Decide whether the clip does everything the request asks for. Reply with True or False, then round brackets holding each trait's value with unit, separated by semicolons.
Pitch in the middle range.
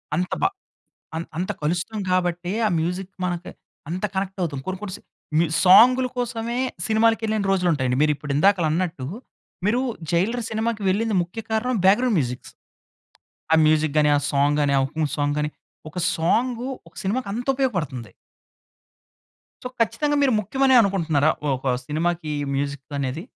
True (180 Hz)